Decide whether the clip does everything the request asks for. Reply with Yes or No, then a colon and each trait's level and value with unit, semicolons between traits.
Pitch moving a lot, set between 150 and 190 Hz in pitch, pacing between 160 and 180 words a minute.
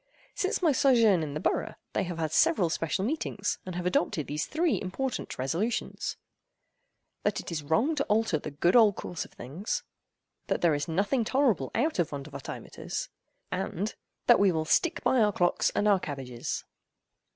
Yes: wide, 6.8 semitones; medium, 185 Hz; average, 175 wpm